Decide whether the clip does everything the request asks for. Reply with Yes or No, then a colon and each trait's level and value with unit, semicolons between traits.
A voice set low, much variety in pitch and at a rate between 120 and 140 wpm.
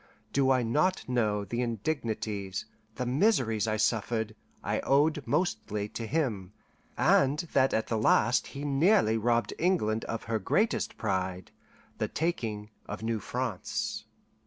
No: low, 115 Hz; average, 4.5 semitones; slow, 135 wpm